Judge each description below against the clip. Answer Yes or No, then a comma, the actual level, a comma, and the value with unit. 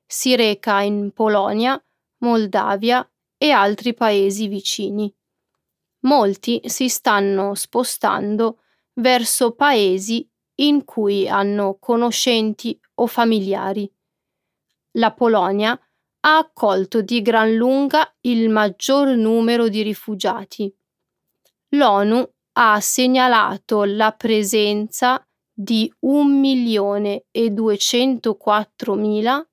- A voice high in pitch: Yes, high, 225 Hz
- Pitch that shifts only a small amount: No, average, 3.3 semitones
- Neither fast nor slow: No, slow, 80 wpm